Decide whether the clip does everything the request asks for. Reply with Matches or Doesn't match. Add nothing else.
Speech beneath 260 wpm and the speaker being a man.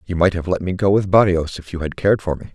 Doesn't match